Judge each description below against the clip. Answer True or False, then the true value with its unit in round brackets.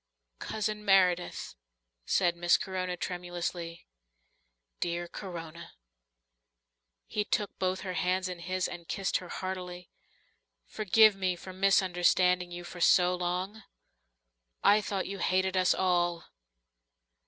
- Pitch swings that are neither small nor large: False (1.3 semitones)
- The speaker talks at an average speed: False (110 wpm)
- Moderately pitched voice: True (180 Hz)